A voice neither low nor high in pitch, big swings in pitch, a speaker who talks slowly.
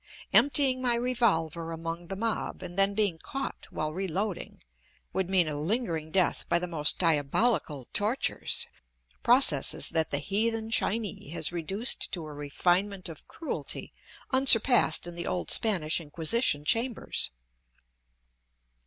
Yes: medium, 180 Hz; wide, 5.9 semitones; slow, 130 wpm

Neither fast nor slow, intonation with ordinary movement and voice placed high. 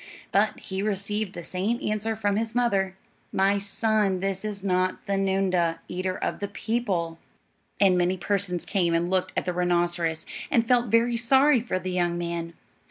Yes: average, 170 wpm; average, 3.1 semitones; high, 195 Hz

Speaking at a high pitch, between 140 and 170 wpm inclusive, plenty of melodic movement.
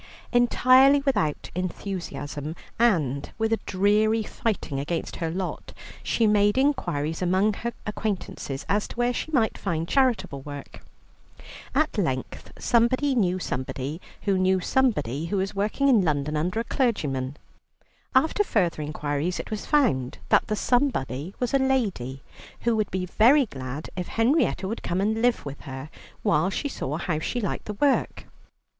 Yes: high, 195 Hz; average, 155 wpm; wide, 7.6 semitones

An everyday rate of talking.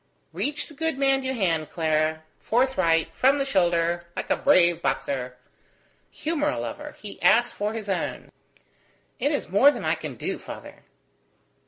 Yes: average, 165 wpm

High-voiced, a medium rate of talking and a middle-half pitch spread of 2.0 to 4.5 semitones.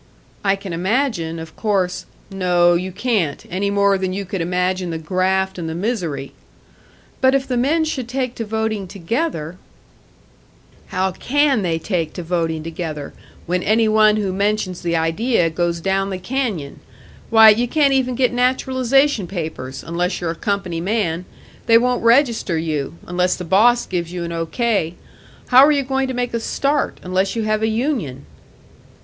No: high, 195 Hz; average, 175 wpm; wide, 5.5 semitones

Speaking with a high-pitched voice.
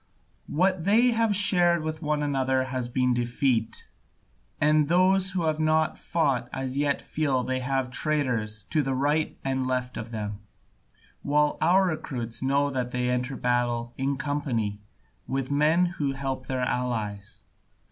No: low, 135 Hz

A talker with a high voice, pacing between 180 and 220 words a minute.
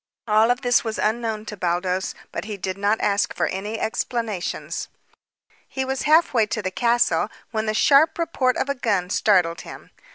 Yes: high, 220 Hz; average, 185 wpm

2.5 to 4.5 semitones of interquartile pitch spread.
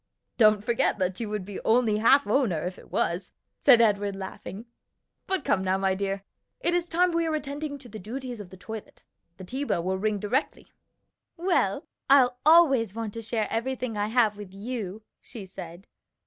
No: average, 5.0 semitones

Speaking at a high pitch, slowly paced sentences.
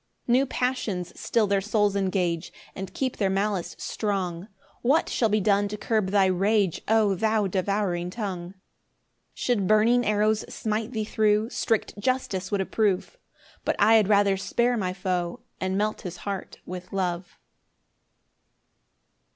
No: high, 205 Hz; average, 150 wpm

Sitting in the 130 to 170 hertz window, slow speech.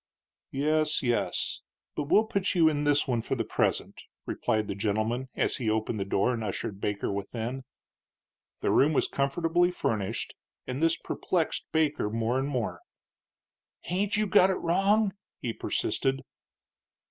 No: low, 135 Hz; average, 150 wpm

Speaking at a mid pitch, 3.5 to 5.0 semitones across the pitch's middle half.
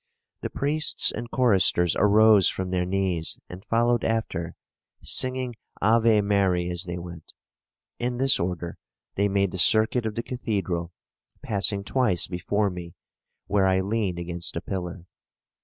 No: low, 100 Hz; average, 4.1 semitones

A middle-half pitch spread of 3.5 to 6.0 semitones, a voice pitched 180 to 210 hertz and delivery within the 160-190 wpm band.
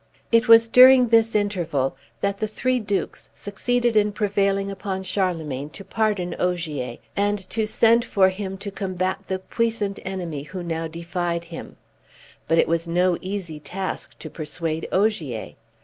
No: average, 3.8 semitones; high, 190 Hz; average, 150 wpm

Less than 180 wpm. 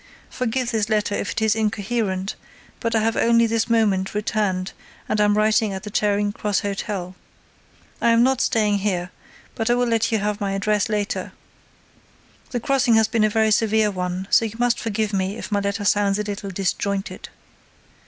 No: average, 185 wpm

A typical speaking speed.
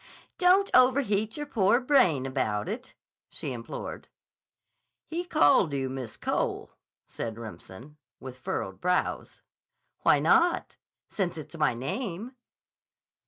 No: slow, 115 wpm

